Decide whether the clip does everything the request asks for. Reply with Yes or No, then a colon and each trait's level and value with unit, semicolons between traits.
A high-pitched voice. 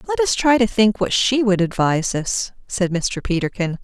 Yes: high, 210 Hz